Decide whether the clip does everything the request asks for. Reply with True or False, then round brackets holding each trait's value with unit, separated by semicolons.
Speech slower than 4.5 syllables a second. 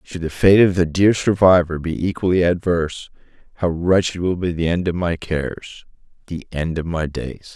False (4.9 syllables/s)